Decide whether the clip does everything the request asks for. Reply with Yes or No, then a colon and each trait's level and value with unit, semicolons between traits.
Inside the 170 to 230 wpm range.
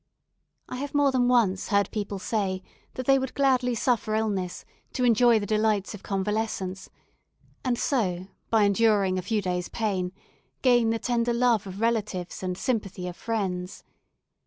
No: average, 160 wpm